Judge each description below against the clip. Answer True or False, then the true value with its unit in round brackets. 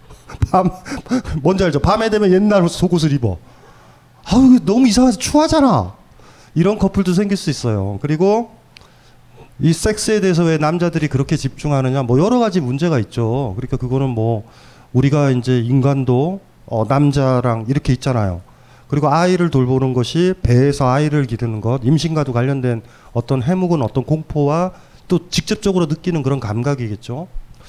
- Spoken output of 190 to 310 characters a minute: False (330 characters per minute)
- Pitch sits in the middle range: True (145 Hz)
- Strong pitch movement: True (6.1 semitones)